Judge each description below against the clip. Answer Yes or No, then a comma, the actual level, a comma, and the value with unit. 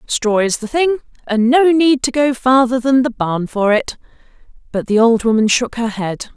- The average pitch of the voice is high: Yes, high, 245 Hz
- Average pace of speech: No, fast, 210 wpm